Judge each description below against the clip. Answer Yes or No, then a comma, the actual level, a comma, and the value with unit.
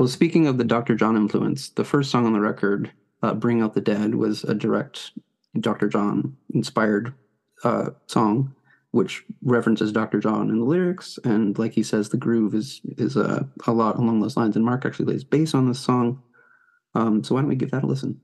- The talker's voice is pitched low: Yes, low, 115 Hz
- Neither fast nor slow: No, fast, 210 wpm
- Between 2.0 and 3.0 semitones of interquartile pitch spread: No, average, 3.8 semitones